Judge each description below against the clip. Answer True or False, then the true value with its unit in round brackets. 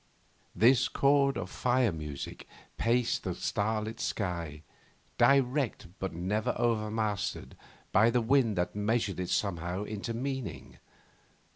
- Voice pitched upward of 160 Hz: False (110 Hz)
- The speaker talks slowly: True (115 wpm)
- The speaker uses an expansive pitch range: False (4.6 semitones)